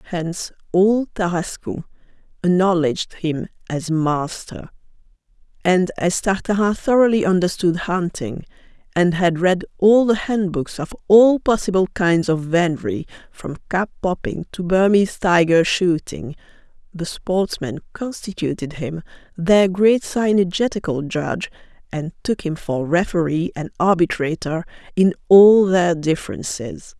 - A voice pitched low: No, medium, 180 Hz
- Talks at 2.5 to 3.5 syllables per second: No, 4.3 syllables/s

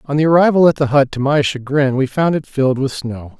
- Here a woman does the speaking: No, male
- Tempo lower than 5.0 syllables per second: No, 5.8 syllables/s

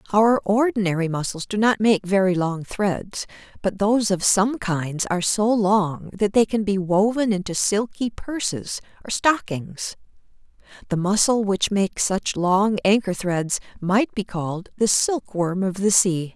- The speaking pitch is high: Yes, high, 200 Hz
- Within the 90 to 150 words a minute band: No, average, 160 wpm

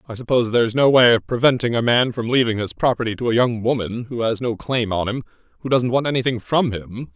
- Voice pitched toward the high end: No, low, 120 Hz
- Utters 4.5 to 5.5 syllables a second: No, 6.1 syllables/s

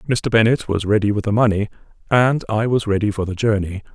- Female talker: No, male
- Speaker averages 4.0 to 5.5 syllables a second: No, 5.9 syllables/s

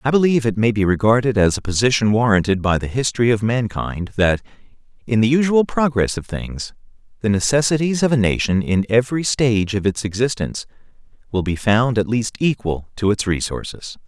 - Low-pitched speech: Yes, low, 115 Hz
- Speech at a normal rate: Yes, average, 180 wpm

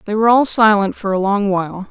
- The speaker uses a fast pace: Yes, fast, 250 wpm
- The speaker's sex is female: Yes, female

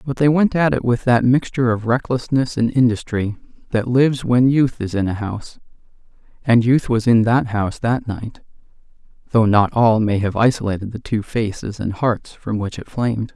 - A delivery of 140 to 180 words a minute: No, average, 195 wpm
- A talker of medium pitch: No, low, 115 Hz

